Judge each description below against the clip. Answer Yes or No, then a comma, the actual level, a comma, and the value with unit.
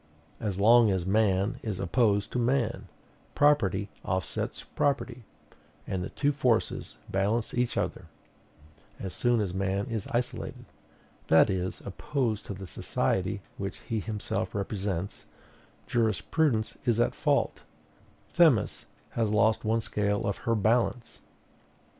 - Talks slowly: Yes, slow, 125 wpm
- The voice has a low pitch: Yes, low, 105 Hz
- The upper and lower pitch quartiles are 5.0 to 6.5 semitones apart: No, average, 3.4 semitones